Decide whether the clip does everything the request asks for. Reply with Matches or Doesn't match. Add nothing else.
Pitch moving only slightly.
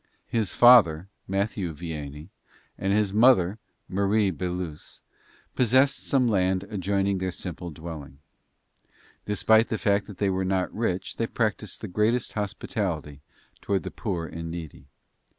Doesn't match